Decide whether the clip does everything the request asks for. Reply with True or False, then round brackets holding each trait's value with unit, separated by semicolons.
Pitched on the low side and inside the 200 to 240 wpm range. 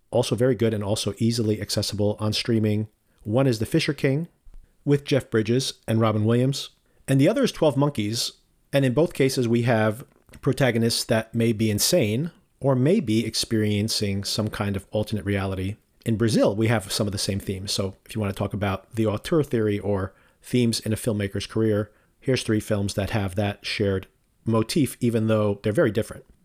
False (110 Hz; 190 wpm)